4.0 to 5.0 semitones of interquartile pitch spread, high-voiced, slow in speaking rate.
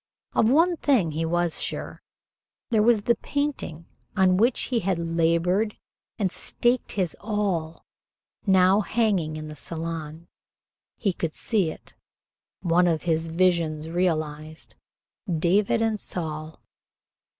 No: average, 4.6 semitones; medium, 175 Hz; slow, 125 wpm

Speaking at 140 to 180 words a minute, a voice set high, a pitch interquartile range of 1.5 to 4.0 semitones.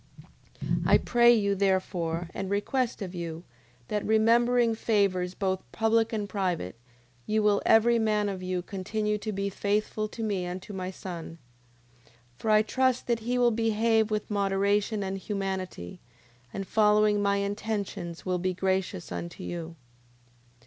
Yes: average, 155 wpm; high, 200 Hz; average, 2.8 semitones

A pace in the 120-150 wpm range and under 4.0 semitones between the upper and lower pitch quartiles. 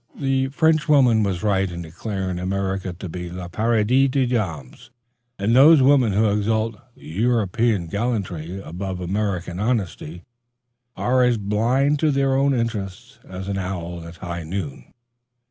No: average, 140 wpm; average, 5.3 semitones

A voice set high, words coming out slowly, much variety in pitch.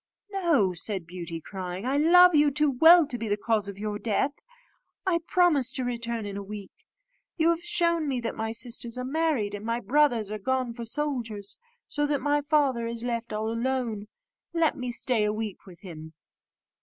No: high, 235 Hz; average, 195 wpm; wide, 5.7 semitones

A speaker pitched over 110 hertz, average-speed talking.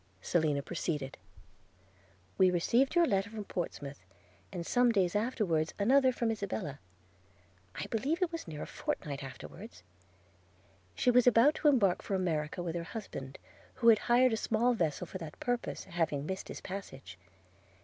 Yes: medium, 185 Hz; average, 160 wpm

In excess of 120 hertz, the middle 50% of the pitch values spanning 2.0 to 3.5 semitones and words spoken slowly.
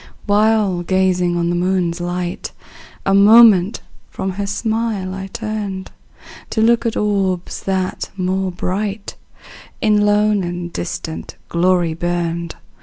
Yes: high, 190 Hz; average, 3.0 semitones; slow, 120 wpm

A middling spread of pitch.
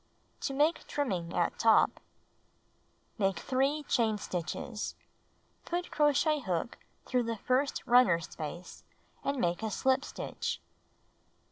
No: wide, 7.0 semitones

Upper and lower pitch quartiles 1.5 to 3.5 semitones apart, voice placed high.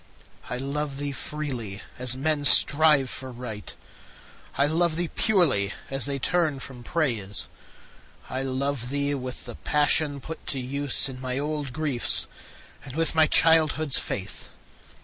No: average, 3.2 semitones; medium, 140 Hz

